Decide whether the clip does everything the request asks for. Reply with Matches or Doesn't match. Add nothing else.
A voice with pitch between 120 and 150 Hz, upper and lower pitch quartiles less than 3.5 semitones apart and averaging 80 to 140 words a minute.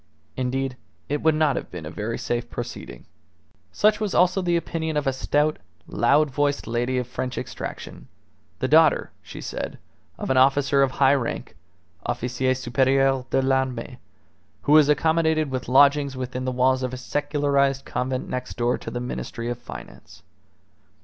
Doesn't match